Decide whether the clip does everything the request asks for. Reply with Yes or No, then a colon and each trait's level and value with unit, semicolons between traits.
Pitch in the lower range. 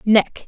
No: high, 210 Hz